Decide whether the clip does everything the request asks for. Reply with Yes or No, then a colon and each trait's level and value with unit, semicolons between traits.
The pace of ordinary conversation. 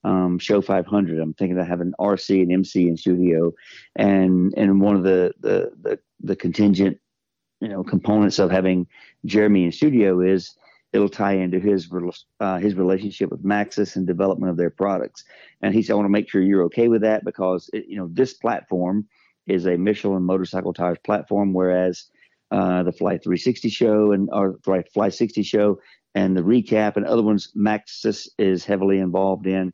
Yes: average, 185 wpm